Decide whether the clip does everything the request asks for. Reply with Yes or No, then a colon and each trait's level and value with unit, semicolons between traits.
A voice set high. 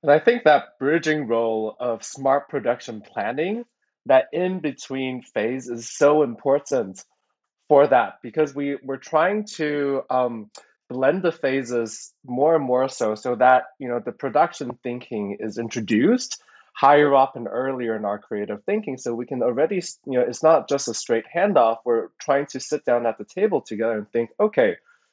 No: low, 135 Hz